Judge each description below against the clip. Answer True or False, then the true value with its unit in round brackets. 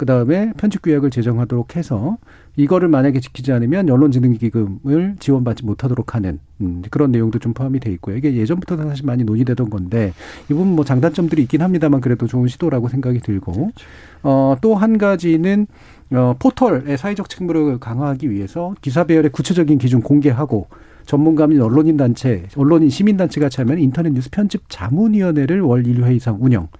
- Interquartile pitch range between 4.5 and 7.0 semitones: True (5.2 semitones)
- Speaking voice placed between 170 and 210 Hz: False (140 Hz)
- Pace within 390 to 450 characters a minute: True (405 characters per minute)